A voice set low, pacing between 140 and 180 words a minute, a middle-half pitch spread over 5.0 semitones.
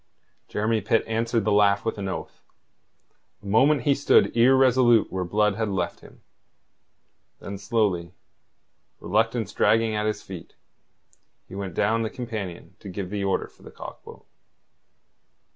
No: low, 105 Hz; average, 145 wpm; narrow, 2.6 semitones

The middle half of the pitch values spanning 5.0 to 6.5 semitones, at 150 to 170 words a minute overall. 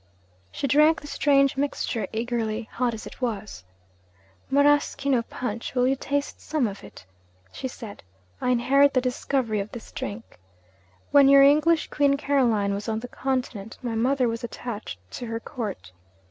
No: average, 3.8 semitones; average, 160 wpm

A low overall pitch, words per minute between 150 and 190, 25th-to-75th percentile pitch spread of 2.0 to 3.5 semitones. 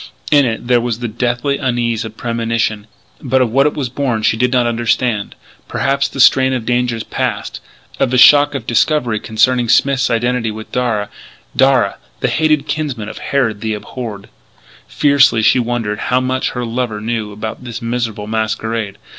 Yes: low, 120 Hz; average, 175 wpm; narrow, 2.5 semitones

